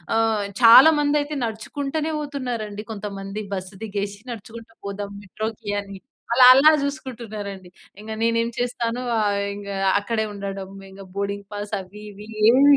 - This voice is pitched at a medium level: No, high, 220 Hz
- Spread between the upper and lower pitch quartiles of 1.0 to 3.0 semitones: No, average, 3.4 semitones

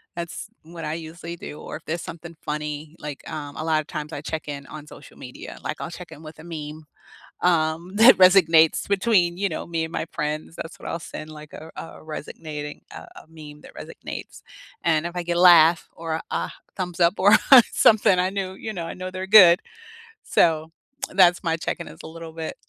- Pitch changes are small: Yes, narrow, 2.2 semitones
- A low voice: No, medium, 165 Hz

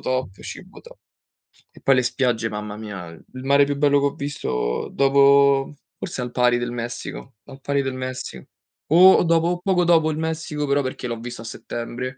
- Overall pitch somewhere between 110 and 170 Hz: Yes, low, 135 Hz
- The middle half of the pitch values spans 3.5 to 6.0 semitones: No, average, 2.8 semitones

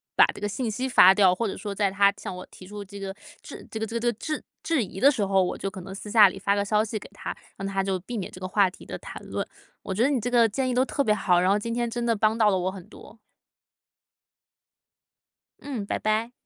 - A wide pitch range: No, average, 3.1 semitones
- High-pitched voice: Yes, high, 205 Hz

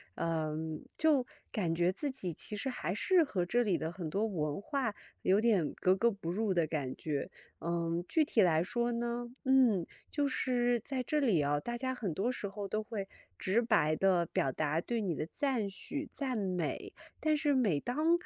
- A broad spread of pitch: Yes, wide, 6.6 semitones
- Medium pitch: No, high, 205 Hz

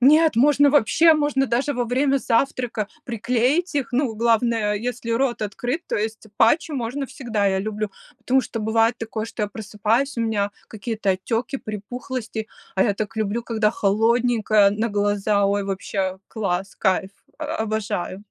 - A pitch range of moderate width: Yes, average, 3.2 semitones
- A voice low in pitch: No, high, 225 Hz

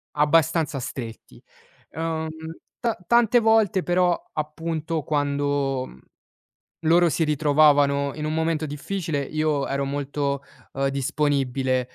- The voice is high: No, medium, 150 Hz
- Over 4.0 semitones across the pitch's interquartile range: No, average, 2.7 semitones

